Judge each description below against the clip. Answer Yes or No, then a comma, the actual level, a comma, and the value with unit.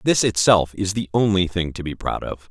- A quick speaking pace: Yes, fast, 240 wpm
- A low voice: Yes, low, 100 Hz